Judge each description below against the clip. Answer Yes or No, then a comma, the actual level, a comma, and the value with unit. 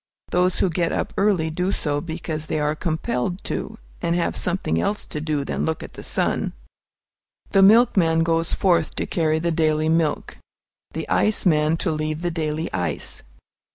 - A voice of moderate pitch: Yes, medium, 160 Hz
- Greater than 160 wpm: Yes, average, 175 wpm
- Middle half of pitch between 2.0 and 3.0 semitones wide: Yes, narrow, 2.4 semitones